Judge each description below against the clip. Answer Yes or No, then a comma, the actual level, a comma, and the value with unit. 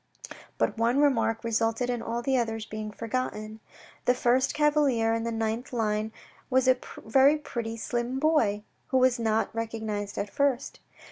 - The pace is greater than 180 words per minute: No, average, 155 wpm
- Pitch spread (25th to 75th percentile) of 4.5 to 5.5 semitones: No, narrow, 2.6 semitones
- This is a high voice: Yes, high, 230 Hz